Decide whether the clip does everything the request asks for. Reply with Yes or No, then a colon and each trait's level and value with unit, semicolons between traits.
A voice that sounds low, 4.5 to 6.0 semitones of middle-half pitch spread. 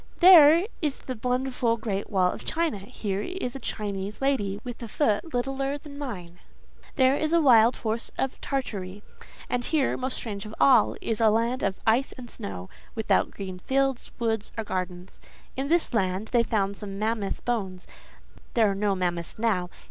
No: high, 225 Hz; average, 5.2 semitones